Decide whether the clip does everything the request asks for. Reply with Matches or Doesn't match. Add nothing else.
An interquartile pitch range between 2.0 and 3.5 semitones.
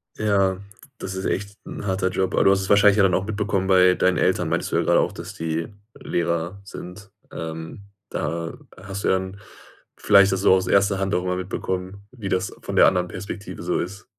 Doesn't match